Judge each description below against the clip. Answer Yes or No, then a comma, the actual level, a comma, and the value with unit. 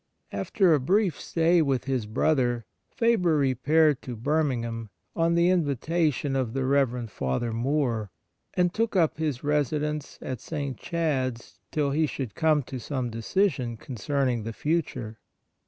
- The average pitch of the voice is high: No, medium, 140 Hz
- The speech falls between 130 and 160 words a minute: Yes, average, 140 wpm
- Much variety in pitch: No, average, 4.7 semitones